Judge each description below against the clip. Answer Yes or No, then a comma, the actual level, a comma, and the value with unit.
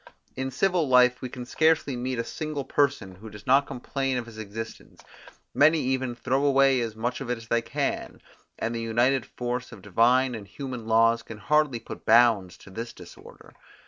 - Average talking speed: Yes, average, 190 wpm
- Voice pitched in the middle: No, low, 125 Hz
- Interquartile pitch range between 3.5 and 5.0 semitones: No, average, 2.8 semitones